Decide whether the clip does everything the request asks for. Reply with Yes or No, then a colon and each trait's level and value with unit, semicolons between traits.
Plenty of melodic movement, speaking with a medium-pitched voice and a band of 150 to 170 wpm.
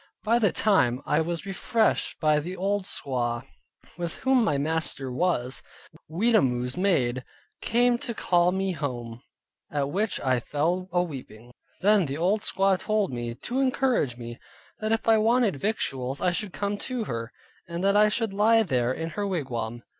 Yes: wide, 8.3 semitones; medium, 175 Hz; average, 165 wpm